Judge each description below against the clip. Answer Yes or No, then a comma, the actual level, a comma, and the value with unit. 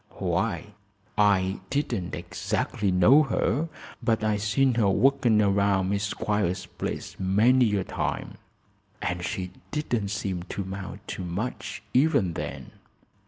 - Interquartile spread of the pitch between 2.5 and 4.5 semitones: Yes, average, 3.9 semitones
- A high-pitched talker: No, low, 105 Hz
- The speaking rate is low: Yes, slow, 125 wpm